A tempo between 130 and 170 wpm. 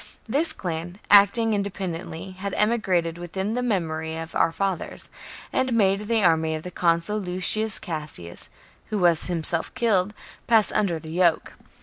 Yes: average, 150 wpm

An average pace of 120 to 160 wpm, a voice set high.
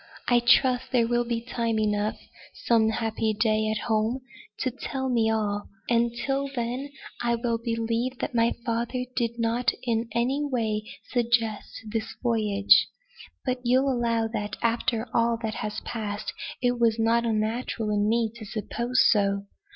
Yes: average, 155 wpm; high, 230 Hz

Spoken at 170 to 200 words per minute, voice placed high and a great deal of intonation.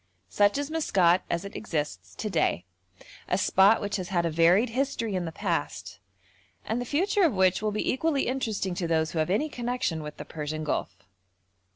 Yes: average, 195 wpm; high, 195 Hz; wide, 6.7 semitones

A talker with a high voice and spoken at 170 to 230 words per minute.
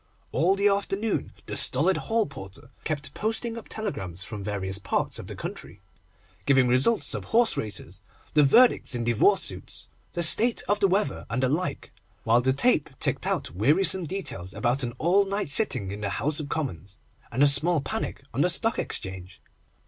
No: medium, 140 Hz; average, 185 wpm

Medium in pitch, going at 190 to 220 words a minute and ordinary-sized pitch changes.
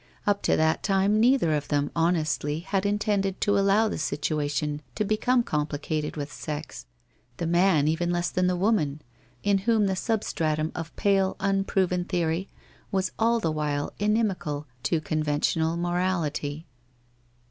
No: medium, 175 Hz; average, 145 wpm; average, 4.3 semitones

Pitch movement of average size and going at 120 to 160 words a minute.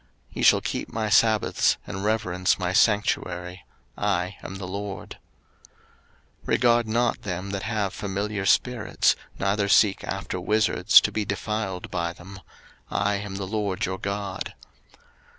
No: narrow, 2.1 semitones; average, 145 wpm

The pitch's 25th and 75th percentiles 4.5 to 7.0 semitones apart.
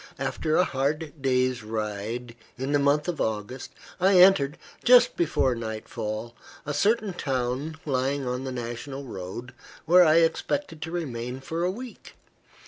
Yes: average, 5.0 semitones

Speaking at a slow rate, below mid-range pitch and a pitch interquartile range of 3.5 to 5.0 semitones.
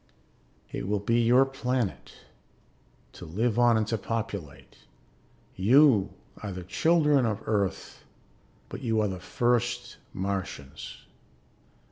Yes: slow, 115 wpm; low, 110 Hz; average, 4.0 semitones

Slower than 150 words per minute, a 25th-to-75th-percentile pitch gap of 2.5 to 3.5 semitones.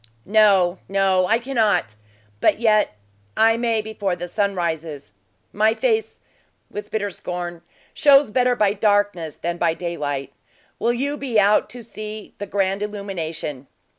No: average, 140 wpm; average, 4.0 semitones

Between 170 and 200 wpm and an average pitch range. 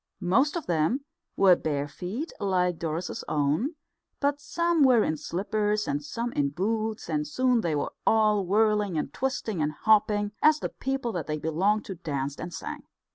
No: average, 175 wpm; wide, 6.5 semitones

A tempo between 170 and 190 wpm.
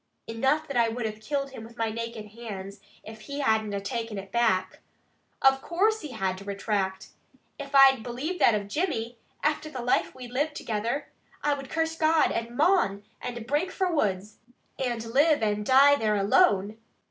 Yes: average, 185 wpm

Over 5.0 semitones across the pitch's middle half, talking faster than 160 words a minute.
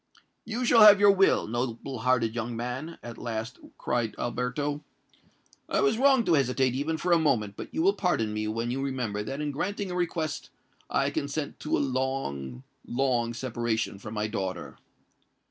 Yes: wide, 5.4 semitones; average, 170 wpm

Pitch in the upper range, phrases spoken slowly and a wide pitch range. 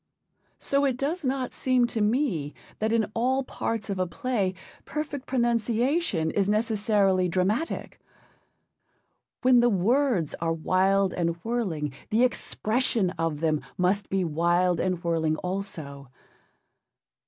Yes: high, 200 Hz; slow, 125 wpm; wide, 5.7 semitones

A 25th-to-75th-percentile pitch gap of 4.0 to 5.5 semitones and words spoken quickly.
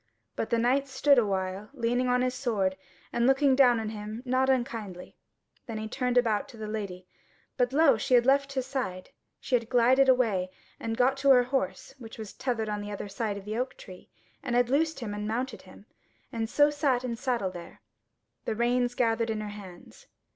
No: average, 3.4 semitones; fast, 210 wpm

